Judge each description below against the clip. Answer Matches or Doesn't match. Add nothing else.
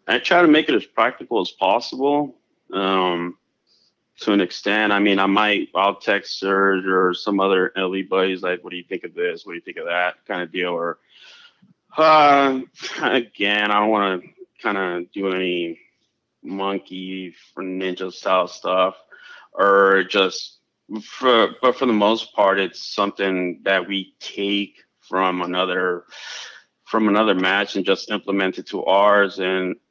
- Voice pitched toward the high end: Doesn't match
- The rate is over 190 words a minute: Doesn't match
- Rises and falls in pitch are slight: Matches